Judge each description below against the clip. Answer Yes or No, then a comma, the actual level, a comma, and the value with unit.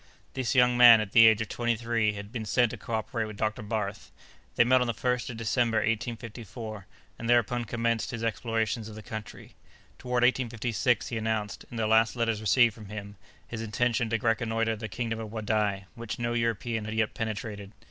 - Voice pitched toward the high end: No, low, 115 Hz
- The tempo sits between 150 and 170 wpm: No, average, 195 wpm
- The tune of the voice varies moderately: No, narrow, 1.6 semitones